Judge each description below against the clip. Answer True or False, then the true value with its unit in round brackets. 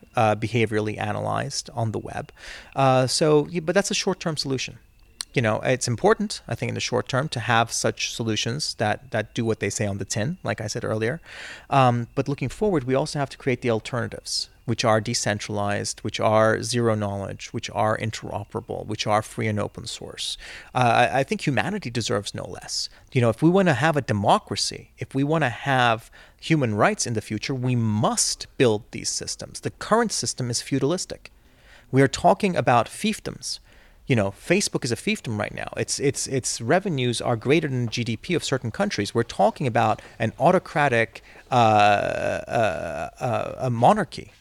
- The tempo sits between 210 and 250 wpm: False (190 wpm)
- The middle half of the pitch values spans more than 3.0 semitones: True (4.3 semitones)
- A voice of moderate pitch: False (120 Hz)